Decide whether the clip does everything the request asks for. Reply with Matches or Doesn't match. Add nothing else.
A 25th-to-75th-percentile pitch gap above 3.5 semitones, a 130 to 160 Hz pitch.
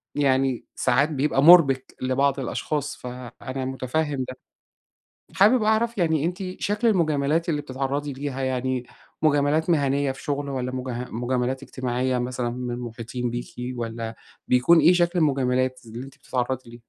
Doesn't match